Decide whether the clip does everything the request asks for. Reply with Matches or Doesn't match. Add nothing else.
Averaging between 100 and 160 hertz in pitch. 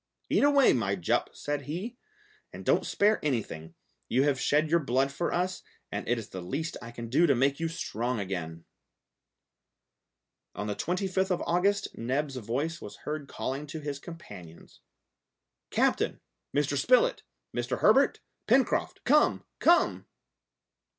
Matches